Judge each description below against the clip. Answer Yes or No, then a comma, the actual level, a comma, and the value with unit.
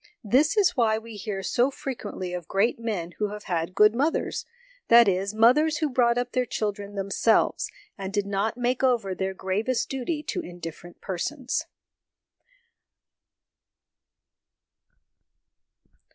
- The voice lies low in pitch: No, high, 220 Hz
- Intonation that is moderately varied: Yes, average, 4.3 semitones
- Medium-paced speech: No, slow, 130 wpm